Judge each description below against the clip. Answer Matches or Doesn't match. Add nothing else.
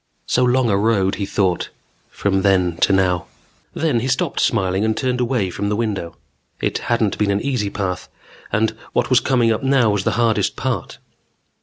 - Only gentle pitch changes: Doesn't match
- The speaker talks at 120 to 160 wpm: Doesn't match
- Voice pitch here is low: Matches